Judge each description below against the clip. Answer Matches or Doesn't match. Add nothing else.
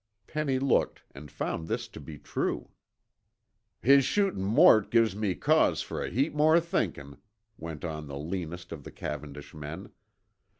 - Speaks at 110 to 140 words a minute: Doesn't match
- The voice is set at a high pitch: Doesn't match